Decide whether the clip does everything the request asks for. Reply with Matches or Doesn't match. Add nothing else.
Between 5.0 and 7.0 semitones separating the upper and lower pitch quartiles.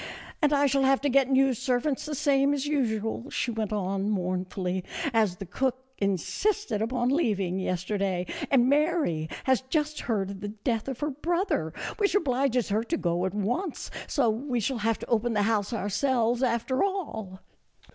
Matches